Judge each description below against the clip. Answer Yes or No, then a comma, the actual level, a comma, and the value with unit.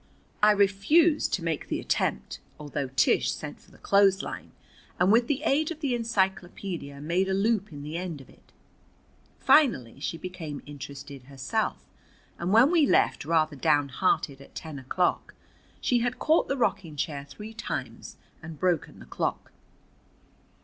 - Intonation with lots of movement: Yes, wide, 7.5 semitones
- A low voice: No, medium, 180 Hz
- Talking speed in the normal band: Yes, average, 155 wpm